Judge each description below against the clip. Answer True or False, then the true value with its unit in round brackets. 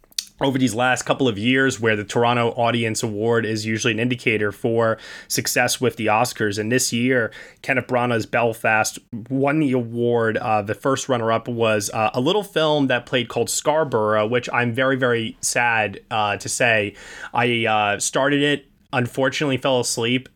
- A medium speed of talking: True (170 wpm)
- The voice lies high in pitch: False (120 Hz)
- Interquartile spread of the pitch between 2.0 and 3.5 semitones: True (2.4 semitones)